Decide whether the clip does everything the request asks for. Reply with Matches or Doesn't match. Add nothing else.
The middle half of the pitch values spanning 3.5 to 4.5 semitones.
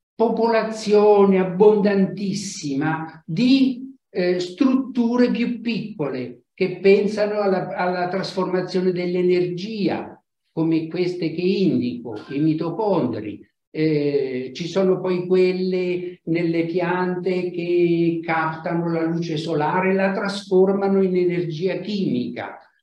Doesn't match